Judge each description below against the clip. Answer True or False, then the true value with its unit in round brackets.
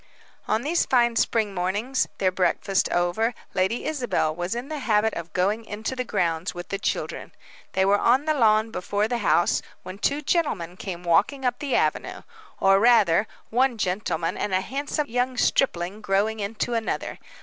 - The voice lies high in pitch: True (215 Hz)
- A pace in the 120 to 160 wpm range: False (170 wpm)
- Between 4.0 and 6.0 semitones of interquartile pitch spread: True (4.7 semitones)